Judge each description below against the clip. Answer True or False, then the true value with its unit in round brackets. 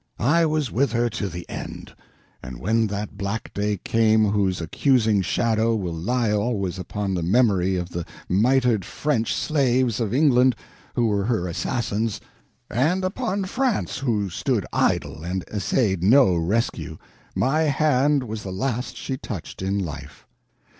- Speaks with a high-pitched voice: False (110 Hz)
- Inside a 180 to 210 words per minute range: False (150 wpm)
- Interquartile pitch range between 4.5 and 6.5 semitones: True (4.8 semitones)